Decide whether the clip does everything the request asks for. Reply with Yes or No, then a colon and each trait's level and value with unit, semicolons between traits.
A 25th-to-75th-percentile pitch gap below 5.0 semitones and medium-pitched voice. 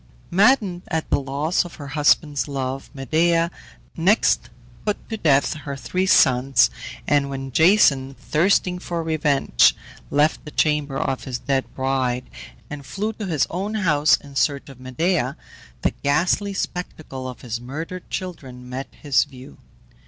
Yes: average, 4.5 semitones; medium, 145 Hz